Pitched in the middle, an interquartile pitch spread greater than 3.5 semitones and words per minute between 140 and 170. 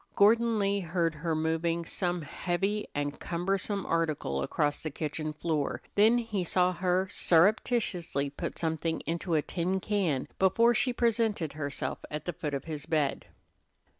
Yes: medium, 170 Hz; average, 4.2 semitones; average, 150 wpm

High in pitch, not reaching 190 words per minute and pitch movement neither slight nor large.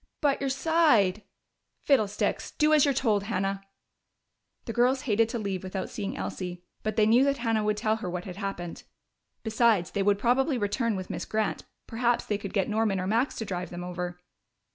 No: high, 215 Hz; average, 195 wpm; average, 3.7 semitones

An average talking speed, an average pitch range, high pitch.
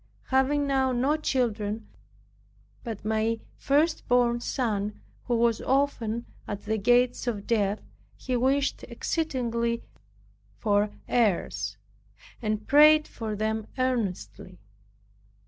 No: slow, 105 wpm; average, 3.5 semitones; high, 235 Hz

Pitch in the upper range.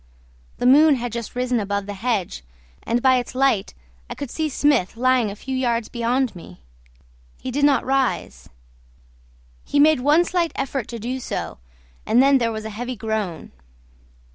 Yes: high, 245 Hz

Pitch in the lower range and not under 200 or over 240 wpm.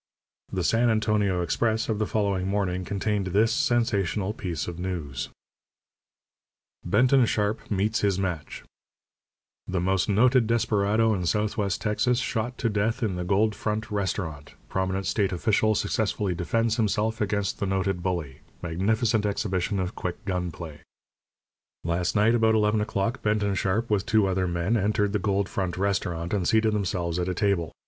No: low, 100 Hz; average, 155 wpm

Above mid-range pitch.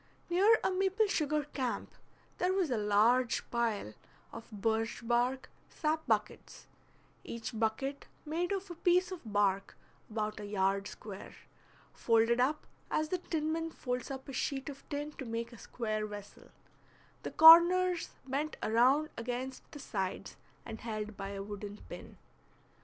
Yes: very high, 250 Hz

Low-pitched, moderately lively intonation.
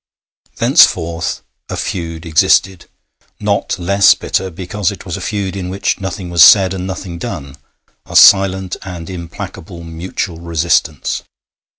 No: very low, 90 Hz; narrow, 2.3 semitones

